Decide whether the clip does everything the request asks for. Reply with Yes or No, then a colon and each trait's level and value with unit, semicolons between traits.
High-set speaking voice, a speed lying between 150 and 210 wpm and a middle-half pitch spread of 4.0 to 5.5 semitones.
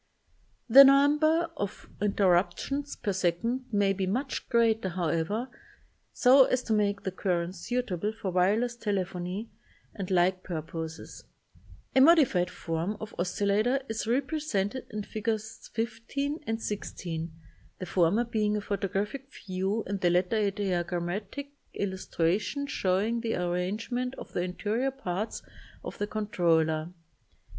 No: high, 205 Hz; slow, 135 wpm; average, 4.5 semitones